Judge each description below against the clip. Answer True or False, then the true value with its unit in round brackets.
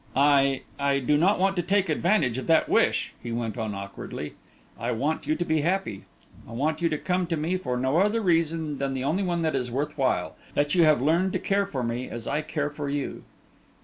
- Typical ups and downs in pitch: True (4.7 semitones)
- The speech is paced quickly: True (230 wpm)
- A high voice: False (150 Hz)